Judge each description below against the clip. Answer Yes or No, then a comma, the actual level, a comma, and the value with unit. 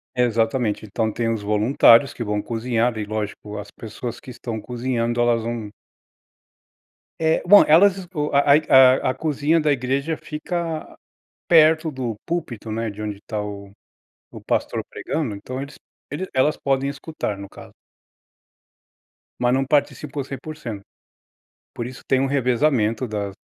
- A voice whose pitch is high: No, low, 125 Hz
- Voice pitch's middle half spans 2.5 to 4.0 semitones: No, average, 4.7 semitones